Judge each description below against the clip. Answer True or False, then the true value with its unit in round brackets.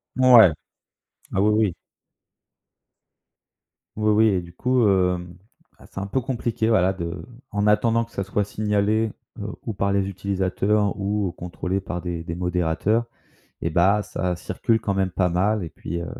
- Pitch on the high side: False (100 Hz)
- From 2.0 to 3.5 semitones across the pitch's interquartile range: True (3.1 semitones)